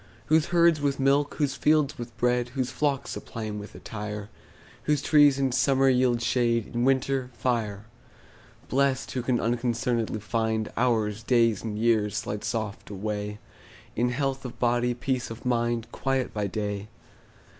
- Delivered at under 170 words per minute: Yes, average, 155 wpm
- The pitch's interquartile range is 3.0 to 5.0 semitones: Yes, average, 3.4 semitones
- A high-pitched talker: No, low, 120 Hz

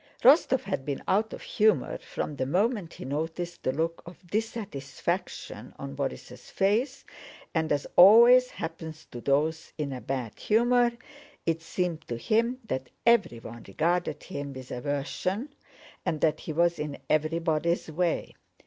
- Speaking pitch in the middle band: Yes, medium, 165 Hz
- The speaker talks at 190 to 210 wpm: No, average, 145 wpm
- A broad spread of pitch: Yes, wide, 6.6 semitones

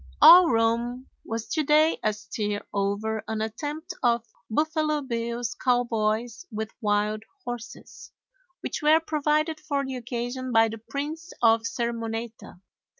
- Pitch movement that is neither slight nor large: Yes, average, 5.0 semitones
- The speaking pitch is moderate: No, high, 235 Hz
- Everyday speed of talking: No, slow, 125 wpm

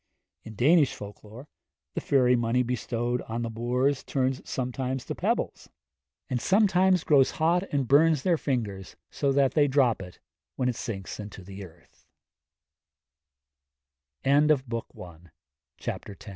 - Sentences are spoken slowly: Yes, slow, 125 wpm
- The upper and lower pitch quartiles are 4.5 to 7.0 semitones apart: No, average, 3.8 semitones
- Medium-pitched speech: No, low, 125 Hz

